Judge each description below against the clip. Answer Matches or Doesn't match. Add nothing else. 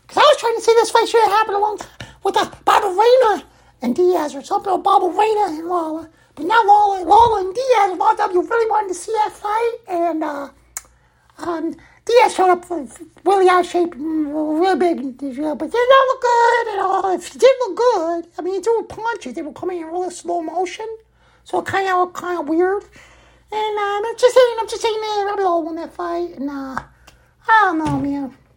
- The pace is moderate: Doesn't match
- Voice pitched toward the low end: Doesn't match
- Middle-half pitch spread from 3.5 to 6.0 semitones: Matches